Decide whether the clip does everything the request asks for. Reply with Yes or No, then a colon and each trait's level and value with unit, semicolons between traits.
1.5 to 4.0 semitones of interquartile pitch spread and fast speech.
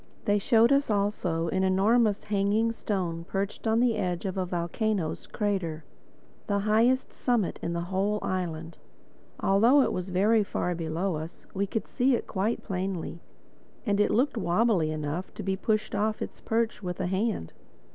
No: average, 3.6 semitones; average, 165 wpm